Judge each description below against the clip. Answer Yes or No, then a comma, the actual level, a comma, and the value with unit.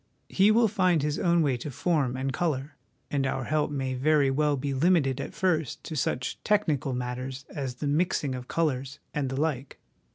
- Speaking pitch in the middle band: Yes, medium, 145 Hz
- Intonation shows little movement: No, average, 3.4 semitones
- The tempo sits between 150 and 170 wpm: No, average, 190 wpm